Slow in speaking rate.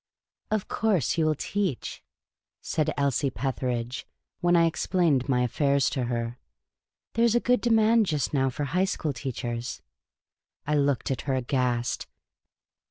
No: average, 160 wpm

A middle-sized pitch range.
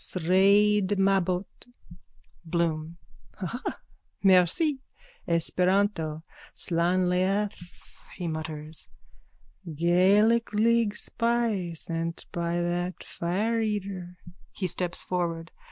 Yes: average, 3.3 semitones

